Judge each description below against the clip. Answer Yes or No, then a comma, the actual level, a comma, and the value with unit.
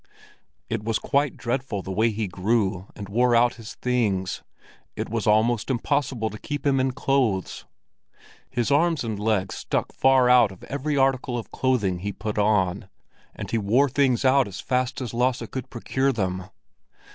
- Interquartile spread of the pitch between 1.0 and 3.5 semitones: No, average, 4.2 semitones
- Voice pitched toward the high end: No, low, 120 Hz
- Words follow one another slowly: No, average, 170 wpm